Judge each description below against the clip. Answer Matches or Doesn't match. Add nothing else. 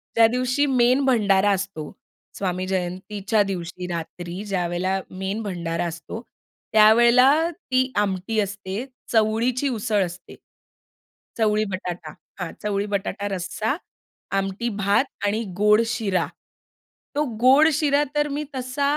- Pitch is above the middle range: Matches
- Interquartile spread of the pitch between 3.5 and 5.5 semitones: Matches